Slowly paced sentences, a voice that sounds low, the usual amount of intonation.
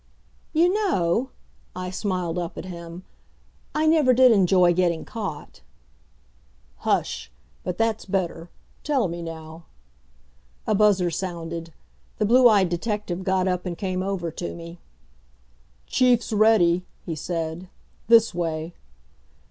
No: slow, 125 wpm; medium, 180 Hz; average, 4.1 semitones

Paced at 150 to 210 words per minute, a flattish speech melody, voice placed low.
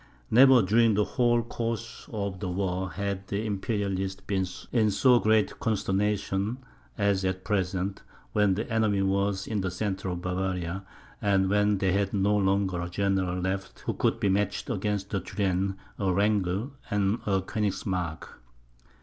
Yes: average, 155 wpm; narrow, 1.8 semitones; low, 100 Hz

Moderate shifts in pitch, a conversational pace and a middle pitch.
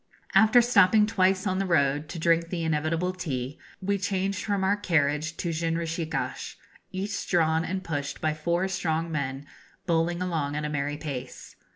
Yes: average, 3.4 semitones; average, 165 wpm; medium, 165 Hz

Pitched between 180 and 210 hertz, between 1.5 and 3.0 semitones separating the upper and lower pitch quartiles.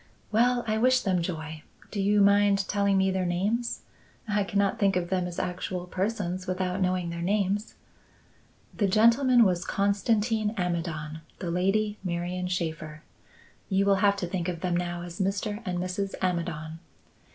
Yes: high, 190 Hz; average, 2.7 semitones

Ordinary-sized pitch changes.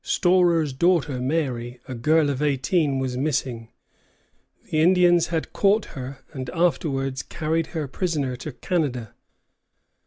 Yes: average, 4.3 semitones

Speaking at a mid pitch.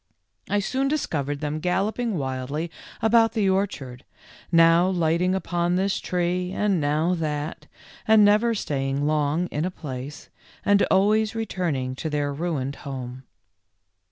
Yes: medium, 170 Hz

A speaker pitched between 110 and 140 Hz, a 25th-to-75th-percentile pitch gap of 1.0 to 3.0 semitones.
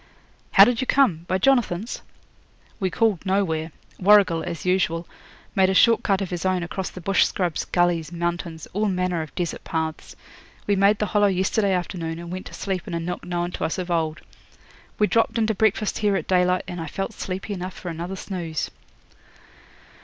No: medium, 185 Hz; narrow, 2.6 semitones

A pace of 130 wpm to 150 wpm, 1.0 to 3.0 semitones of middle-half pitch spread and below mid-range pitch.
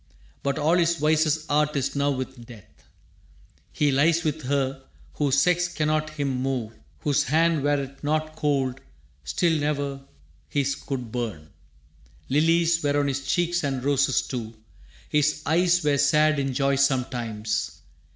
No: average, 140 wpm; narrow, 2.5 semitones; medium, 145 Hz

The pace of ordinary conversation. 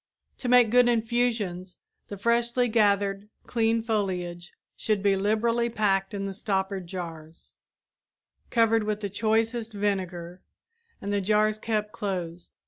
No: slow, 125 wpm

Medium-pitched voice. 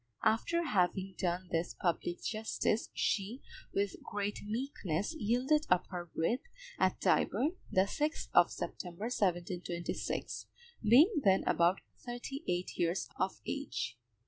No: high, 200 Hz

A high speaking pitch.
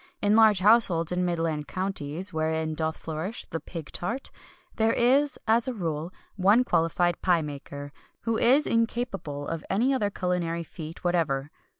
No: medium, 180 Hz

